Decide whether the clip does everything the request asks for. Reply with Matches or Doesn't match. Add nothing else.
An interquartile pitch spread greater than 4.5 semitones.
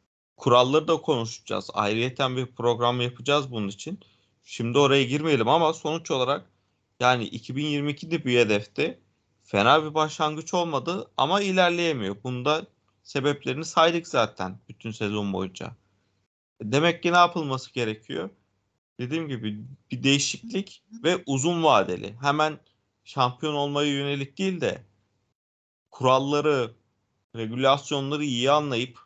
Matches